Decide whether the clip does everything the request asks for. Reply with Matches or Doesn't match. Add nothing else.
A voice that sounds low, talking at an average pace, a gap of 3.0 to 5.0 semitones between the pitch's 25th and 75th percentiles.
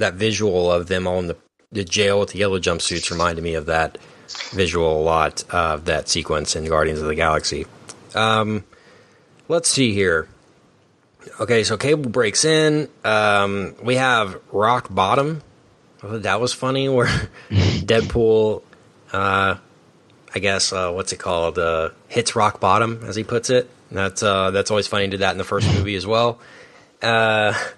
Matches